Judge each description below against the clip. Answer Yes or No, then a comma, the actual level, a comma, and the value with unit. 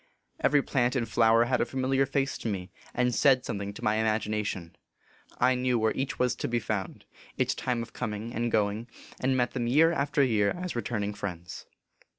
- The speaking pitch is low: Yes, low, 120 Hz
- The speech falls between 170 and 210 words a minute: Yes, average, 190 wpm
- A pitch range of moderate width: Yes, average, 3.2 semitones